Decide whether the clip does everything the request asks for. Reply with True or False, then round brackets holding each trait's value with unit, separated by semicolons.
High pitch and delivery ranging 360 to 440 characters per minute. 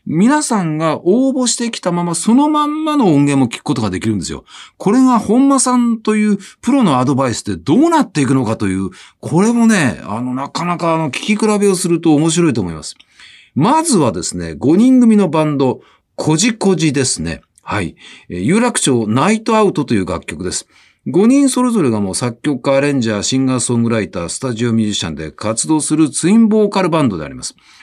False (160 Hz; 405 characters per minute)